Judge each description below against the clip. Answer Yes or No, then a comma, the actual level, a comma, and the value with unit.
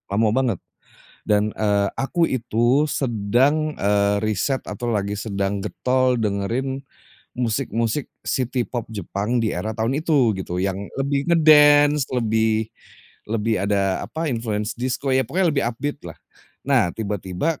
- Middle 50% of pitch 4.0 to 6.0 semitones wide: Yes, average, 4.6 semitones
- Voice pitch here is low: Yes, low, 115 Hz